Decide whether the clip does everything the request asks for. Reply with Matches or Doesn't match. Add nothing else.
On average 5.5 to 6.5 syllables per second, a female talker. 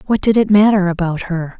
Matches